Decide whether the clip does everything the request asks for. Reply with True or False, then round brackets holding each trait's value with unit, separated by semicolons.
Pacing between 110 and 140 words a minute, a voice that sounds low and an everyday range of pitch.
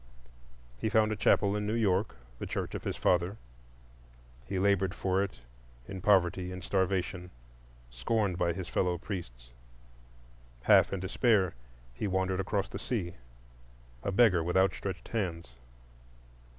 False (135 wpm; 95 Hz; 2.2 semitones)